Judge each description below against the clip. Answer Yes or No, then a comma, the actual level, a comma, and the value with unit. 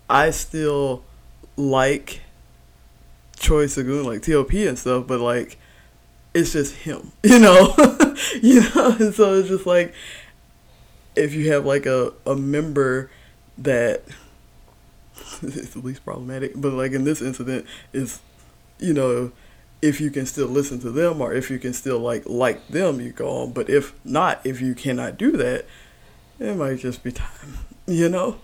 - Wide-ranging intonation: No, average, 4.7 semitones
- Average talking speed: Yes, average, 165 wpm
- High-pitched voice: No, low, 135 Hz